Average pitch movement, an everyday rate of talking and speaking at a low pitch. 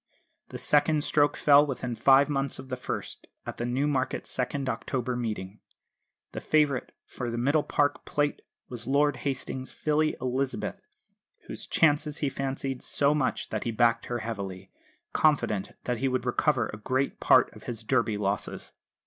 Yes: average, 3.3 semitones; average, 160 wpm; low, 130 Hz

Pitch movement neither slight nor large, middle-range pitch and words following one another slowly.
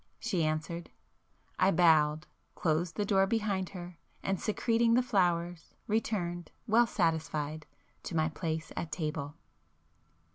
Yes: average, 4.0 semitones; medium, 175 Hz; slow, 115 wpm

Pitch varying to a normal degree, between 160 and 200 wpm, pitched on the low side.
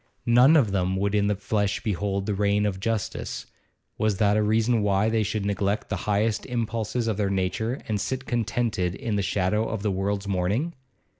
No: narrow, 2.2 semitones; average, 195 wpm; low, 105 Hz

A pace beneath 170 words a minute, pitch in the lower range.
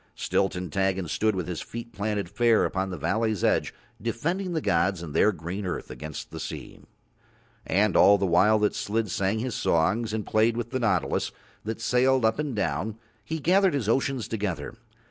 No: average, 185 wpm; low, 105 Hz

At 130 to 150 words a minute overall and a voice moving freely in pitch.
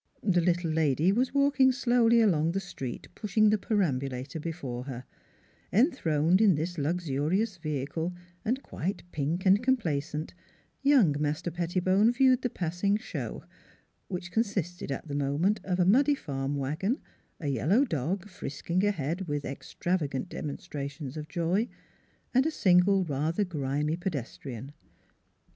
Yes: slow, 135 wpm; wide, 5.8 semitones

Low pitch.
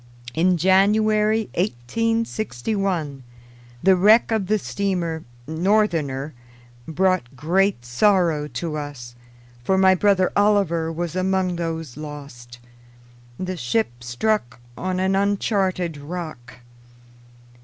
No: medium, 180 Hz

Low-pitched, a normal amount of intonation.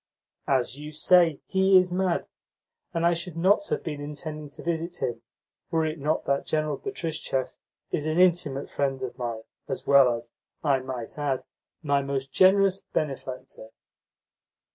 No: medium, 150 Hz; average, 4.1 semitones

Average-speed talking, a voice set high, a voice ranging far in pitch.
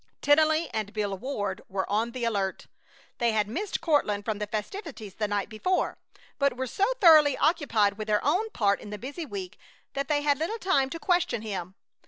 Yes: average, 195 wpm; high, 245 Hz; wide, 7.1 semitones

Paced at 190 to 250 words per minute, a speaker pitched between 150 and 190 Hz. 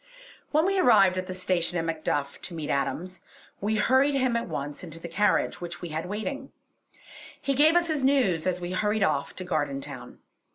Yes: average, 195 wpm; medium, 185 Hz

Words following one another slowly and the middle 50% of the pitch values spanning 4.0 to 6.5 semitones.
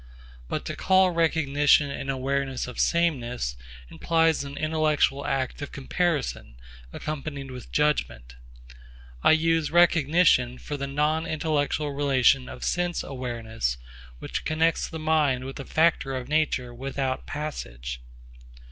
No: slow, 125 wpm; average, 3.3 semitones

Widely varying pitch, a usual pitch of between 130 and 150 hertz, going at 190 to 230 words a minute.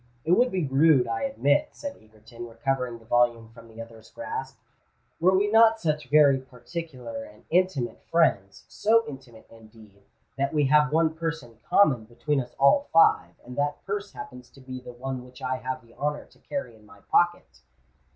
No: wide, 5.7 semitones; low, 135 Hz; average, 180 wpm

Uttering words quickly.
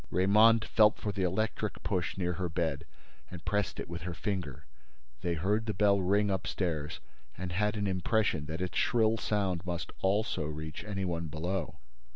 No: average, 175 wpm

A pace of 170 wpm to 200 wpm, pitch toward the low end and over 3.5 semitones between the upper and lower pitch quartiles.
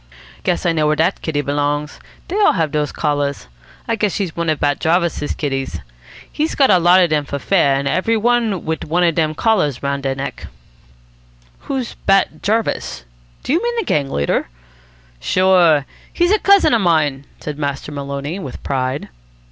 No: average, 180 wpm; medium, 160 Hz; wide, 5.5 semitones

